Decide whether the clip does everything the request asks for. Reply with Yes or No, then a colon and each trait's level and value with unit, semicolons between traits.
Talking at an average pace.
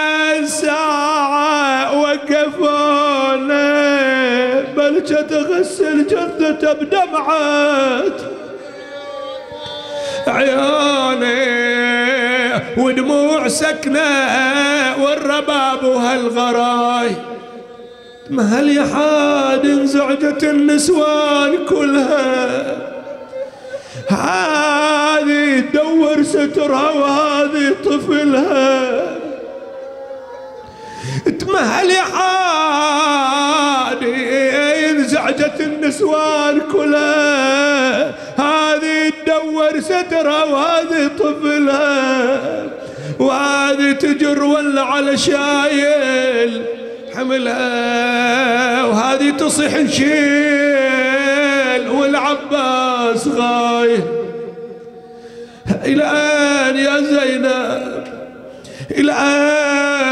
No: slow, 45 wpm